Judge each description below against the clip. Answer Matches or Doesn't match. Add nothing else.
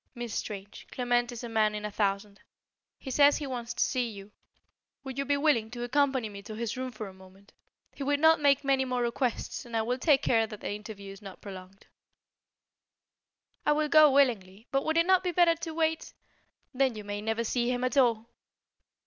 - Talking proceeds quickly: Matches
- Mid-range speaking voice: Doesn't match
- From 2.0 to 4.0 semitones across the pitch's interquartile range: Doesn't match